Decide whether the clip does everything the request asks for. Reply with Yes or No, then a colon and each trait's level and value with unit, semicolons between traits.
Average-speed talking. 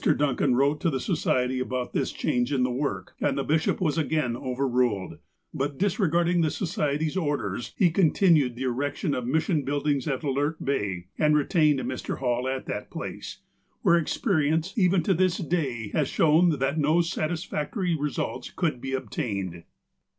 Yes: average, 165 wpm